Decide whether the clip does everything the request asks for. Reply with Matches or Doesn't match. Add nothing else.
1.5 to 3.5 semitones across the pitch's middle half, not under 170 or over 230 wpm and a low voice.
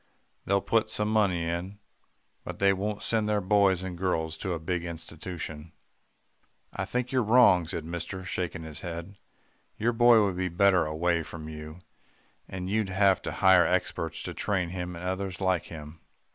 Matches